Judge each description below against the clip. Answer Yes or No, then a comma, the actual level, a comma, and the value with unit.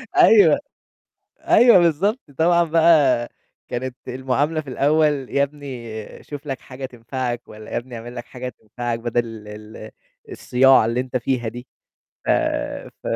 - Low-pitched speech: Yes, low, 130 Hz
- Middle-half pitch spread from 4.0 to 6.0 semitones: No, average, 3.6 semitones